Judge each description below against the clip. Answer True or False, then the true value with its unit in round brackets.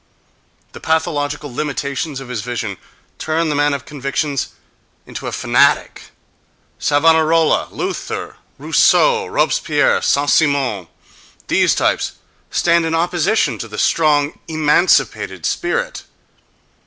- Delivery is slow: True (100 wpm)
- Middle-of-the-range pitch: True (150 Hz)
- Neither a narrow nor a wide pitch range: True (3.0 semitones)